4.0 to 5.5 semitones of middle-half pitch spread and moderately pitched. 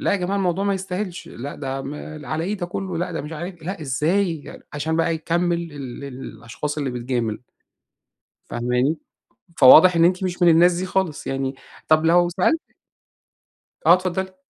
Yes: average, 4.5 semitones; medium, 165 Hz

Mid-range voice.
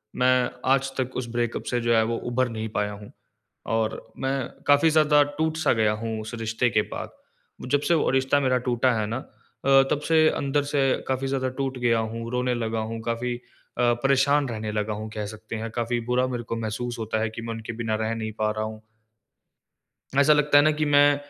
No: low, 120 Hz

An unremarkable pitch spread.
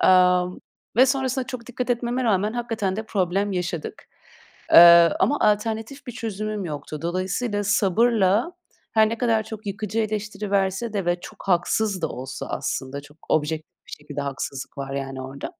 Yes: average, 4.6 semitones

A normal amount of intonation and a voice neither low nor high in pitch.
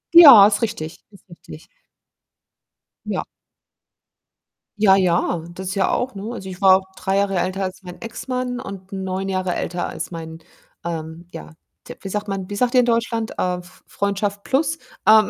No: average, 3.1 semitones; high, 195 Hz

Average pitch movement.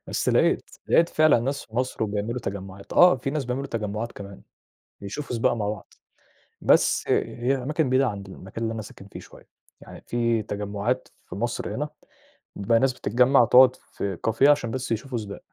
Yes: average, 4.2 semitones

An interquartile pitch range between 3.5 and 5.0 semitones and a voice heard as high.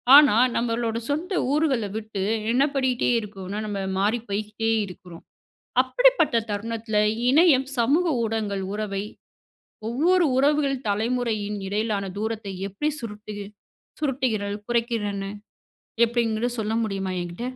Yes: average, 4.0 semitones; high, 225 Hz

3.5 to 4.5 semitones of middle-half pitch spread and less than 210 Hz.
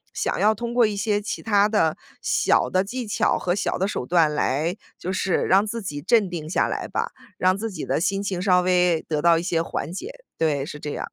Yes: average, 3.8 semitones; medium, 185 Hz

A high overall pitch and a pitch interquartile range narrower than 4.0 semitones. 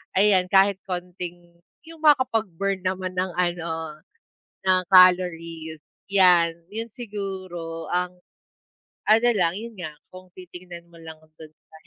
No: medium, 180 Hz; narrow, 2.5 semitones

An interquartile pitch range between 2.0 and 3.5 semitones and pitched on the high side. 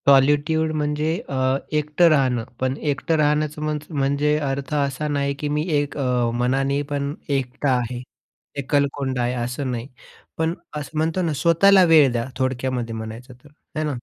No: narrow, 2.5 semitones; medium, 140 Hz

